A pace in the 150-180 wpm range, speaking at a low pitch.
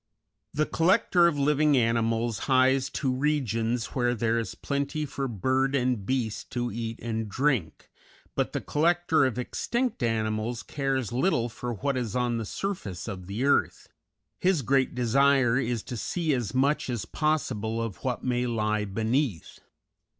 Yes: average, 155 wpm; low, 125 Hz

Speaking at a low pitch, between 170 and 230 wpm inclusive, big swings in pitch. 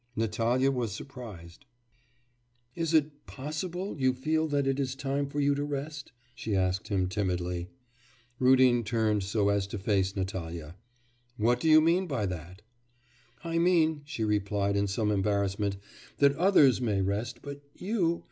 No: low, 120 Hz; average, 150 wpm; wide, 6.3 semitones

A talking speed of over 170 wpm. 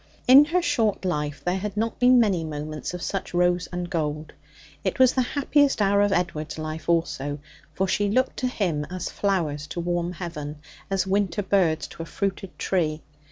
Yes: average, 185 wpm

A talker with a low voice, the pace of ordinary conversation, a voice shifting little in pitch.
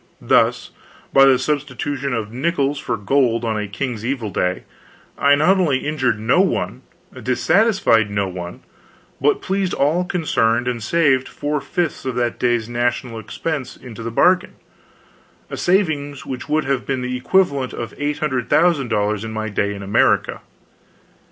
No: low, 130 Hz; average, 150 wpm; average, 4.7 semitones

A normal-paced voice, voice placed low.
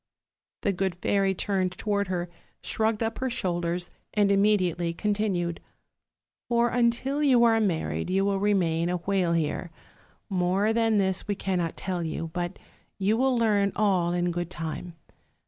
No: average, 150 wpm; high, 195 Hz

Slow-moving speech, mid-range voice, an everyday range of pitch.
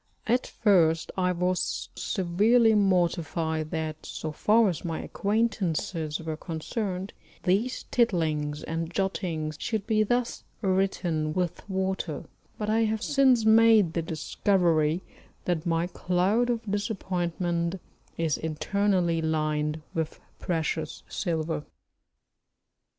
Yes: slow, 110 wpm; medium, 180 Hz; average, 4.3 semitones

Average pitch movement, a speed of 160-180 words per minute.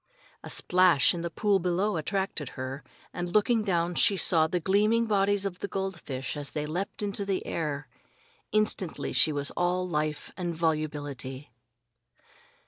No: average, 4.6 semitones; average, 150 wpm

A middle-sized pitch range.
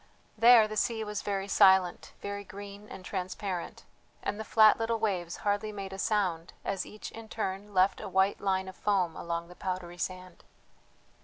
No: narrow, 2.3 semitones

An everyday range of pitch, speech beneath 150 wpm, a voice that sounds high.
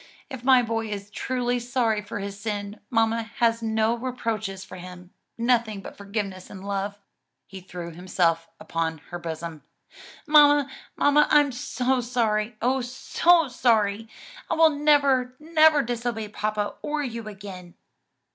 Yes: average, 4.1 semitones; average, 140 wpm; high, 225 Hz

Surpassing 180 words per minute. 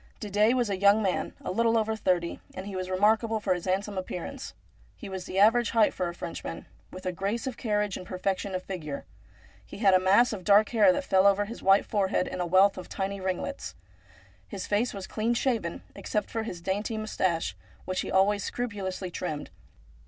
Yes: fast, 205 wpm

